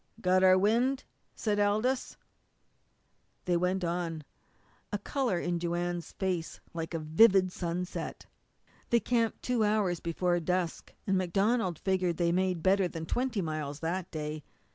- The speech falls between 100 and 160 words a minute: Yes, average, 140 wpm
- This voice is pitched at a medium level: Yes, medium, 180 Hz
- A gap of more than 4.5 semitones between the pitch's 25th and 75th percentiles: No, average, 3.3 semitones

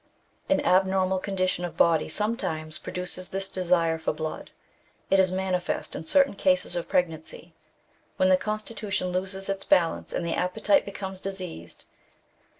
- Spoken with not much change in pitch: Yes, narrow, 2.1 semitones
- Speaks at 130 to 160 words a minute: Yes, average, 145 wpm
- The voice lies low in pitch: No, medium, 185 Hz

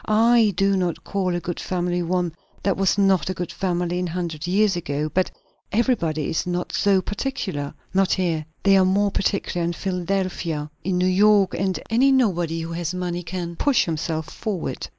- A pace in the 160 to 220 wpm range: Yes, average, 175 wpm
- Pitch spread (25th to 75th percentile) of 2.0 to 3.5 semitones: Yes, narrow, 2.4 semitones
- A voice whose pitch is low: No, medium, 180 Hz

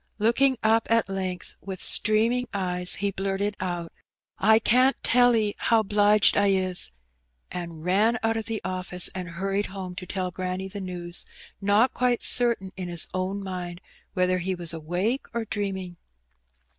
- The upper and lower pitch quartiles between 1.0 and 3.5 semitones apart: Yes, average, 3.2 semitones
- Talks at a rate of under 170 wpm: Yes, average, 160 wpm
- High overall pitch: Yes, high, 195 Hz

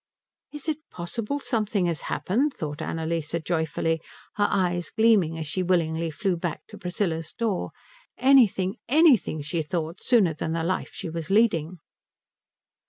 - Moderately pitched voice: Yes, medium, 175 Hz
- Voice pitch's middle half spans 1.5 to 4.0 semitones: No, average, 4.8 semitones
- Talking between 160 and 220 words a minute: No, average, 145 wpm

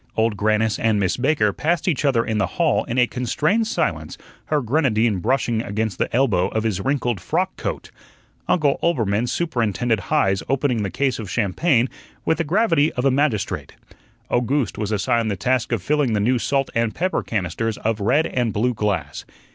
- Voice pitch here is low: Yes, low, 115 Hz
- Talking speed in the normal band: Yes, average, 180 wpm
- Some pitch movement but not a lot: Yes, average, 4.6 semitones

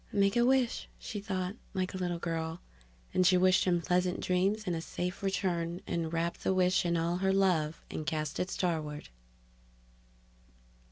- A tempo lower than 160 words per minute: No, average, 170 wpm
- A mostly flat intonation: Yes, narrow, 2.2 semitones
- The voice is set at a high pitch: No, medium, 180 Hz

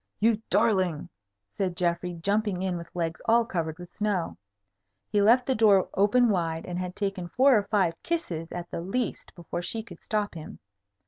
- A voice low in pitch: No, high, 190 Hz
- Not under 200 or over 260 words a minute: No, average, 180 wpm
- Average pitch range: Yes, average, 3.7 semitones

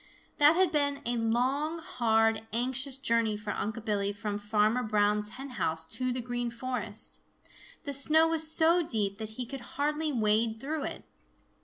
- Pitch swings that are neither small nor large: Yes, average, 4.8 semitones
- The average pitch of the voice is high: Yes, high, 240 Hz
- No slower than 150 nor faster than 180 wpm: Yes, average, 165 wpm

